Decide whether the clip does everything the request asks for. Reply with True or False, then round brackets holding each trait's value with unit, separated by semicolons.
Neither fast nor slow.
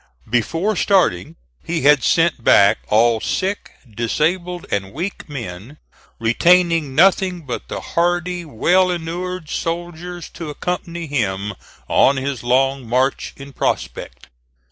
False (120 wpm)